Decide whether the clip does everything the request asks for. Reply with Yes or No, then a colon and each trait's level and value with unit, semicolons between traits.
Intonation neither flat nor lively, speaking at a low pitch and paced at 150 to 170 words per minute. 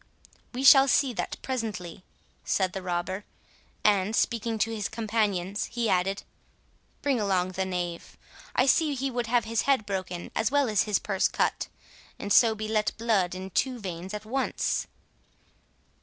No: average, 4.0 semitones; high, 210 Hz; average, 160 wpm